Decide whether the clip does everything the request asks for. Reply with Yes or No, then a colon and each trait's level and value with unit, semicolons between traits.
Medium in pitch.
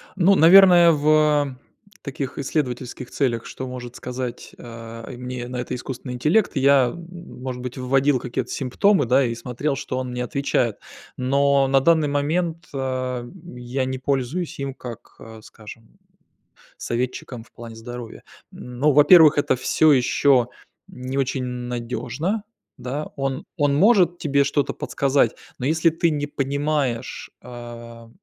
No: low, 130 Hz